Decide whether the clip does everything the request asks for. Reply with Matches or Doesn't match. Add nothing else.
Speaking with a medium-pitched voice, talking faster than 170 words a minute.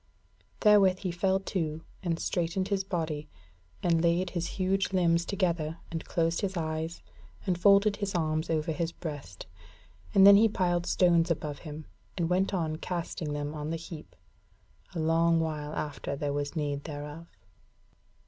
Doesn't match